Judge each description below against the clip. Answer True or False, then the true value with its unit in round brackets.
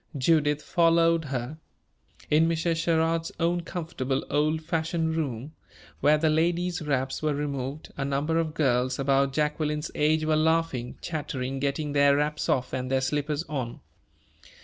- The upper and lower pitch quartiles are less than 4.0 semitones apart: True (2.8 semitones)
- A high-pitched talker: False (150 Hz)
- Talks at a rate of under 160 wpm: True (145 wpm)